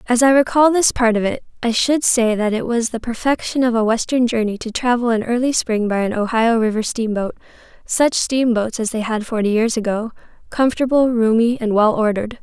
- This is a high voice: Yes, high, 230 Hz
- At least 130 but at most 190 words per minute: No, average, 200 wpm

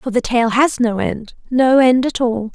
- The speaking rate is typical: No, fast, 235 wpm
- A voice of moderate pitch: No, high, 240 Hz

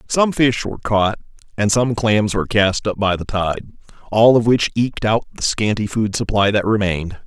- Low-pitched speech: Yes, low, 105 Hz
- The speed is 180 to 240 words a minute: Yes, average, 200 wpm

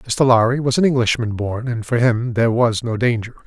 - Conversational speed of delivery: No, fast, 225 wpm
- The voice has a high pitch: No, low, 120 Hz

